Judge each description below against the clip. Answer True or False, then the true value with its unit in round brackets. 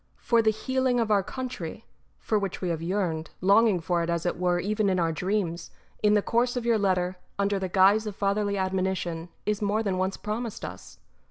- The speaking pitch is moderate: False (195 Hz)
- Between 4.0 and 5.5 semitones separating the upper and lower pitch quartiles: False (3.0 semitones)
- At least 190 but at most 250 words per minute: True (205 wpm)